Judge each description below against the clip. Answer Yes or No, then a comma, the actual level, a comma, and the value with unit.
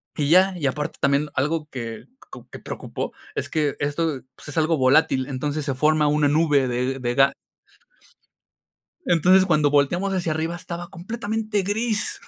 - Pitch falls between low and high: Yes, medium, 150 Hz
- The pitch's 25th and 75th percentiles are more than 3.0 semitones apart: Yes, average, 3.9 semitones